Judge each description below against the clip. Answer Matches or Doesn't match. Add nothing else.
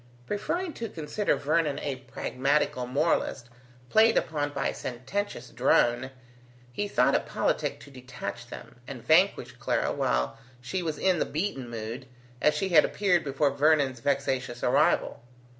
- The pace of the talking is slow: Doesn't match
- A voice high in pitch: Doesn't match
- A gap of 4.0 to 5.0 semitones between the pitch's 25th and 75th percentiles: Matches